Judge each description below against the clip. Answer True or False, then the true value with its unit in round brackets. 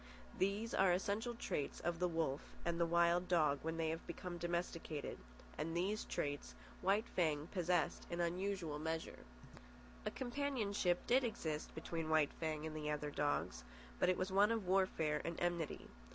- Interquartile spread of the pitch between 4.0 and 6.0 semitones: False (3.2 semitones)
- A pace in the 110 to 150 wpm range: False (165 wpm)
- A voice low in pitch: False (170 Hz)